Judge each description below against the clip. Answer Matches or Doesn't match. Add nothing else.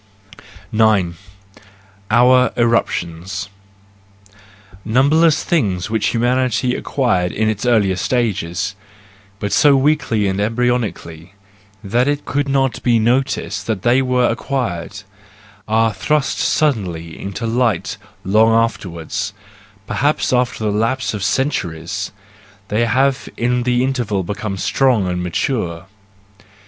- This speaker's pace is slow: Matches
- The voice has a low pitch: Matches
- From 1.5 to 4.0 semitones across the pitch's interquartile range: Doesn't match